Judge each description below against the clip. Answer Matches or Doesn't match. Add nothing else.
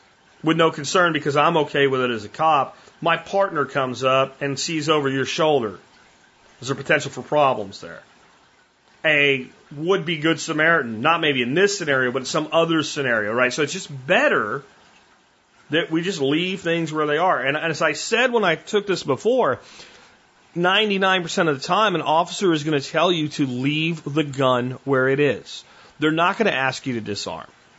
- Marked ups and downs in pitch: Doesn't match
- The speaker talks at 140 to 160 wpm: Doesn't match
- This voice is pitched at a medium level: Matches